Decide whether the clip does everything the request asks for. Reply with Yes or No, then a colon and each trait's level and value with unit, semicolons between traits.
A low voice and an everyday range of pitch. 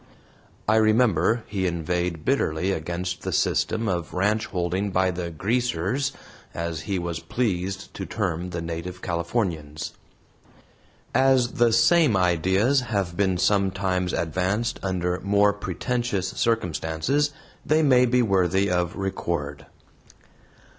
Yes: very low, 95 Hz; average, 4.3 semitones